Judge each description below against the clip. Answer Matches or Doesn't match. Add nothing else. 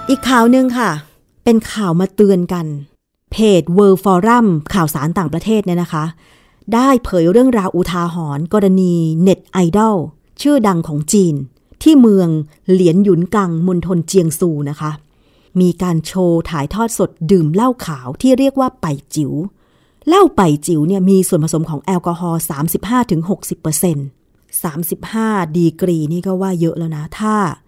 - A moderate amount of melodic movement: Matches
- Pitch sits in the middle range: Matches